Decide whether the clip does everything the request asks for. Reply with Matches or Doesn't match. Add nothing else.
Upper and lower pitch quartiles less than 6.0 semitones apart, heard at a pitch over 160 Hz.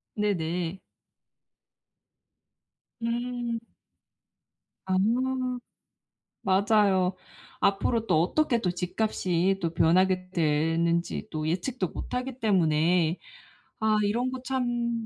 Matches